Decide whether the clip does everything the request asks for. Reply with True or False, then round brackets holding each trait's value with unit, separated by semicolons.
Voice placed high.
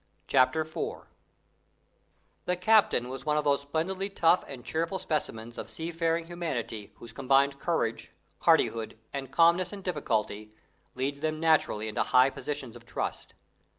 False (145 Hz)